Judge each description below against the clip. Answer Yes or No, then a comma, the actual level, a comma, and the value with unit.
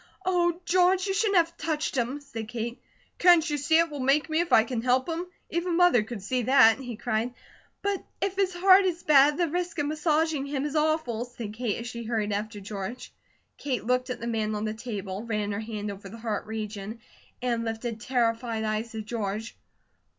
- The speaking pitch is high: Yes, high, 245 Hz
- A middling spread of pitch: No, wide, 6.4 semitones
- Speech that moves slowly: No, fast, 205 wpm